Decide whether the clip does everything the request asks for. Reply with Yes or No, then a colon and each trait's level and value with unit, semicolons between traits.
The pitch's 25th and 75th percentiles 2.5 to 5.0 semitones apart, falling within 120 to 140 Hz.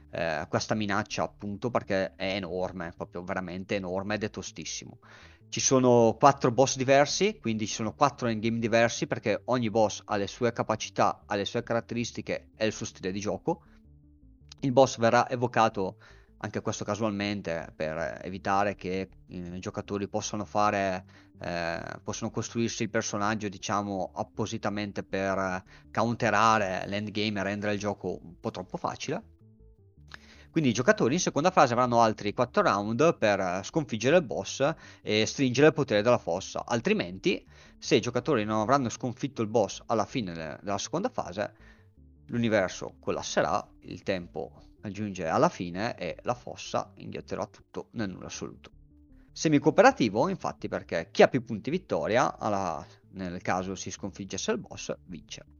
No: average, 3.5 semitones; low, 105 Hz